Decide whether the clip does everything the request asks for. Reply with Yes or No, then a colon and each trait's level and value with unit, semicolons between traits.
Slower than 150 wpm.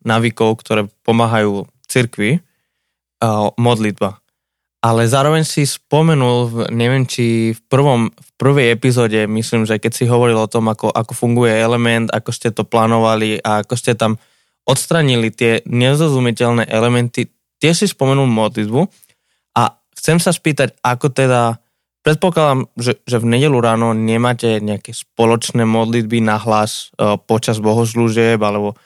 Yes: average, 135 wpm